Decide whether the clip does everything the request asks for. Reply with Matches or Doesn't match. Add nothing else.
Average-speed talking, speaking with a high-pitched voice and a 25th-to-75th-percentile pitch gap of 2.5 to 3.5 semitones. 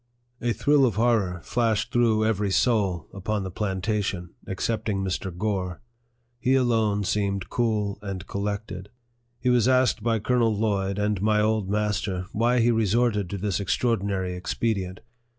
Doesn't match